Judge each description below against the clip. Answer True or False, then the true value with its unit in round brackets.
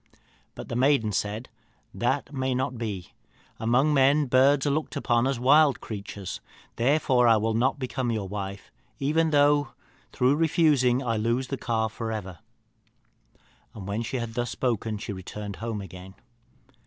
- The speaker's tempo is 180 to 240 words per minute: False (160 wpm)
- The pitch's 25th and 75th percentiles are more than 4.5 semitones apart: False (4.0 semitones)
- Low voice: True (120 Hz)